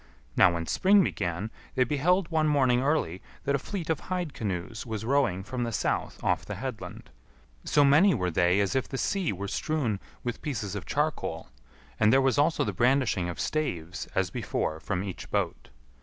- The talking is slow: No, average, 185 wpm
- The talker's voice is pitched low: Yes, low, 120 Hz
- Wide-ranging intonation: Yes, wide, 7.7 semitones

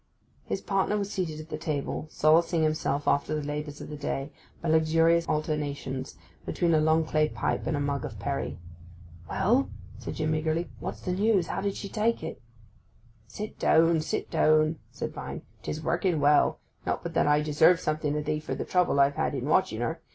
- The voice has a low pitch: No, medium, 155 Hz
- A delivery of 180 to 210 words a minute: Yes, average, 190 wpm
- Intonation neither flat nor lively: No, narrow, 2.1 semitones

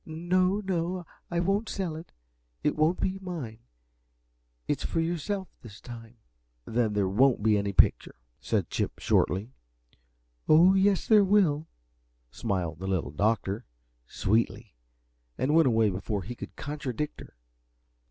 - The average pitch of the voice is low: No, medium, 145 Hz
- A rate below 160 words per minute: Yes, average, 140 wpm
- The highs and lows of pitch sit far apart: Yes, wide, 8.6 semitones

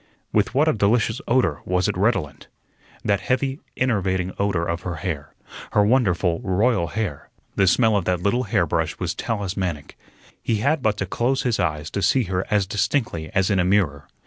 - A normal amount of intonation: Yes, average, 4.1 semitones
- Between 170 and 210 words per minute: Yes, average, 180 wpm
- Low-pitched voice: Yes, low, 100 Hz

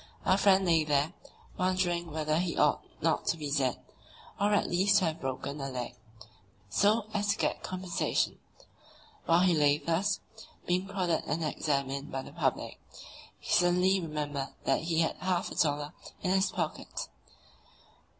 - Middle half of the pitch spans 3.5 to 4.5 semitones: Yes, average, 4.2 semitones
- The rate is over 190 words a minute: No, average, 160 wpm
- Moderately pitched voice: Yes, medium, 165 Hz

